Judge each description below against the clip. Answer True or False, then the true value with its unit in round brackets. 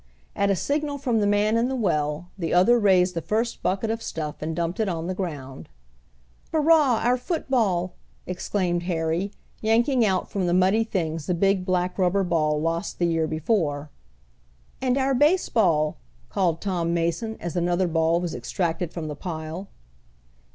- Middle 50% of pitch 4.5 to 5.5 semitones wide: True (5.0 semitones)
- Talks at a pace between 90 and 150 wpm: False (165 wpm)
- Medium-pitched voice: True (180 Hz)